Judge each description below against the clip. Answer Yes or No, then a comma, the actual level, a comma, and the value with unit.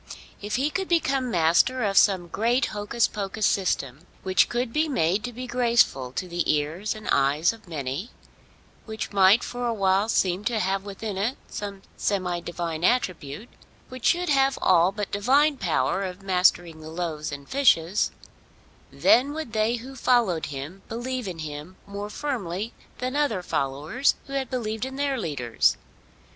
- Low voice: No, high, 205 Hz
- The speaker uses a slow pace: No, average, 160 wpm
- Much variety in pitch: Yes, wide, 6.1 semitones